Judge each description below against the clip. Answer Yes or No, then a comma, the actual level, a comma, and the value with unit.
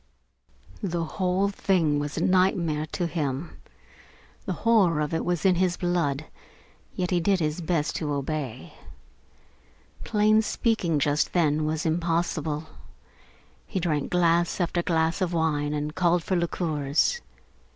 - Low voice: No, medium, 170 Hz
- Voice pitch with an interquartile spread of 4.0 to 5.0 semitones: No, average, 2.9 semitones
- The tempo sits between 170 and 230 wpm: No, slow, 135 wpm